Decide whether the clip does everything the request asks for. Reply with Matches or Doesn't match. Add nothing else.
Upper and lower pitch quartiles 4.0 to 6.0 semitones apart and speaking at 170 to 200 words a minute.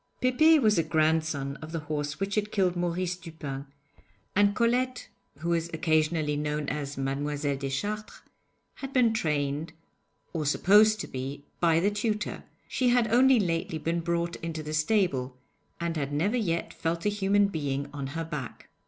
Doesn't match